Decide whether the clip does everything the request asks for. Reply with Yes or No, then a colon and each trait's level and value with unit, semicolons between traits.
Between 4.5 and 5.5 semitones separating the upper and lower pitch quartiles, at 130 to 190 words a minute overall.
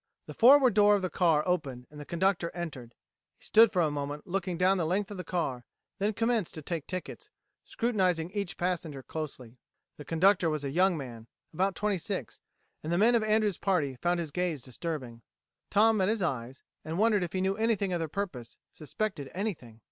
No: average, 5.0 semitones; average, 200 wpm